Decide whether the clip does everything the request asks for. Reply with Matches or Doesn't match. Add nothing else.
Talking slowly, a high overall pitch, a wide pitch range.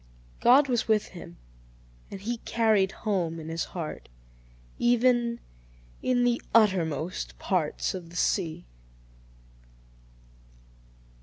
Matches